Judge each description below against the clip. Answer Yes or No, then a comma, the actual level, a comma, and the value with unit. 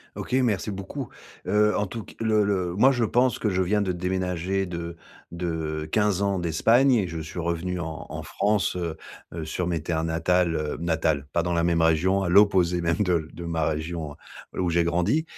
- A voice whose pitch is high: No, very low, 90 Hz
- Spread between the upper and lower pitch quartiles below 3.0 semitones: No, average, 3.3 semitones